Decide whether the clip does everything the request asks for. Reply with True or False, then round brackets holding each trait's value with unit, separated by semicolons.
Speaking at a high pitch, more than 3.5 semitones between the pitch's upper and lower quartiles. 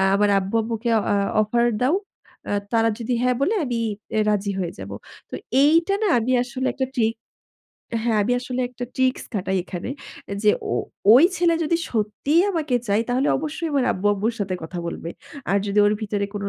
True (230 Hz; 4.2 semitones)